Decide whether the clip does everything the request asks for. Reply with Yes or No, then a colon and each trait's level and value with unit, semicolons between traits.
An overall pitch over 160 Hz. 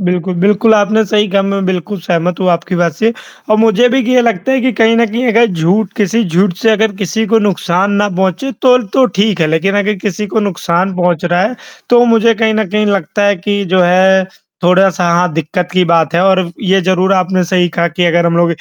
Yes: high, 190 Hz